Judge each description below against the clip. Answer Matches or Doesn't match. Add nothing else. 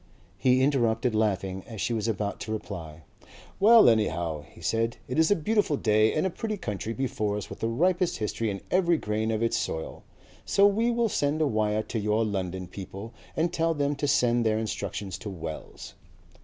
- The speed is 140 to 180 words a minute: Doesn't match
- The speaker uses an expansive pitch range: Matches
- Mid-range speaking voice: Doesn't match